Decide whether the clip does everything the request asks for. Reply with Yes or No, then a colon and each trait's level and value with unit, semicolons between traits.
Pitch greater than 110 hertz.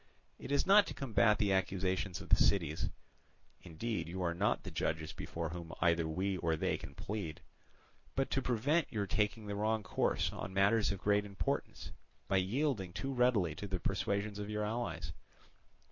No: low, 100 Hz